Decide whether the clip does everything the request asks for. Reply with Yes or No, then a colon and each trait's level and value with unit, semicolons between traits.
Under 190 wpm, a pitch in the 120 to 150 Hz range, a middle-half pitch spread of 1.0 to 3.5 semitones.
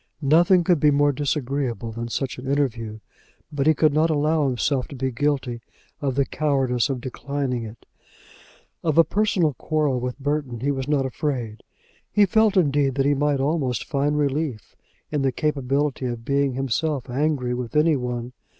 Yes: average, 170 wpm; medium, 140 Hz; average, 2.9 semitones